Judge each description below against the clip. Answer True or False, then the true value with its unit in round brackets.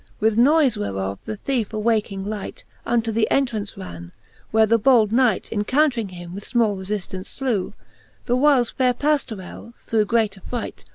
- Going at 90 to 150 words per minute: False (160 wpm)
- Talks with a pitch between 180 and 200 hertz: False (220 Hz)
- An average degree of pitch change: True (3.6 semitones)